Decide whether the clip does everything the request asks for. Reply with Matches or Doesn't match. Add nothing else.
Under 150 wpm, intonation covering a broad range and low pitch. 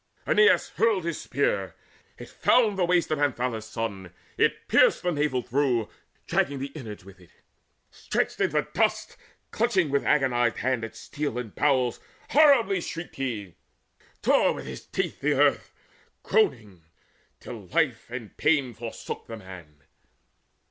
Matches